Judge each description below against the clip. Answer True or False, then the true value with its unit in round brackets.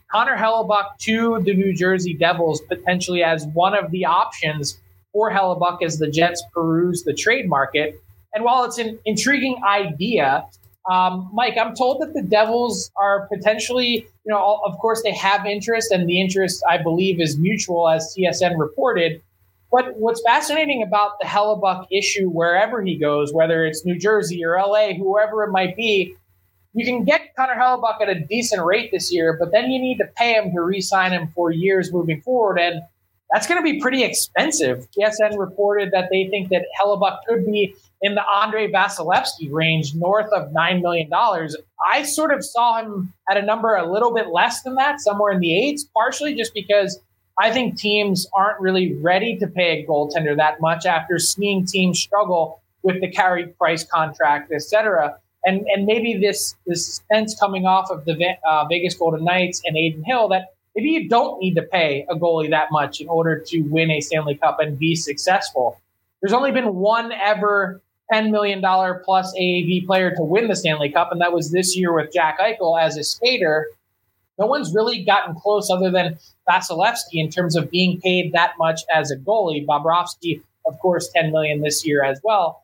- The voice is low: False (185 Hz)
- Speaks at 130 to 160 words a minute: False (185 wpm)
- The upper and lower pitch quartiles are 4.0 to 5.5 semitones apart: True (4.4 semitones)